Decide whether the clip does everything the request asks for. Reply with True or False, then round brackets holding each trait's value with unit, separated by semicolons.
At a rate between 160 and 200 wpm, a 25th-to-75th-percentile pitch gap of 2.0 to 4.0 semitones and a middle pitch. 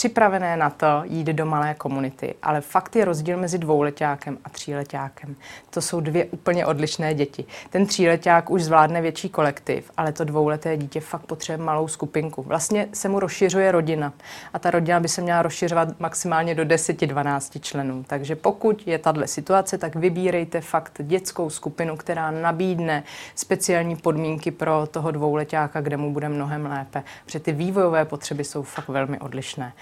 True (165 wpm; 2.5 semitones; 160 Hz)